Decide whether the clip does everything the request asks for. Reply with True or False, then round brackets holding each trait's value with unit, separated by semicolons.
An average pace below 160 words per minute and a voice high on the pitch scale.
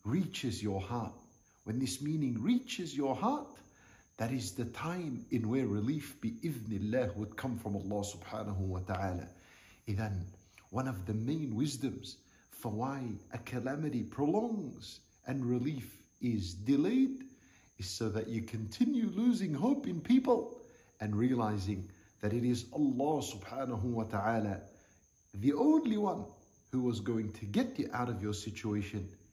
False (145 wpm; 120 Hz)